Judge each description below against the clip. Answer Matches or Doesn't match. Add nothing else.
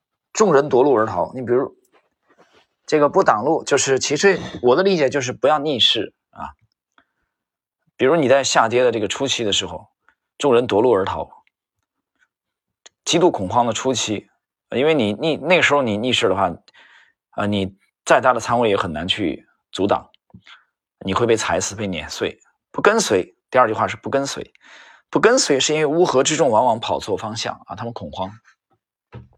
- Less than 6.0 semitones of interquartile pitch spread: Doesn't match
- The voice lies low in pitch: Matches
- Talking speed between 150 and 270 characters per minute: Matches